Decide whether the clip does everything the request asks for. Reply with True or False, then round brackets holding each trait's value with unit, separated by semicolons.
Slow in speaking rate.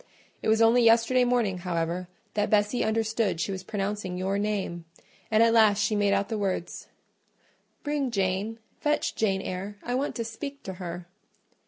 False (165 wpm)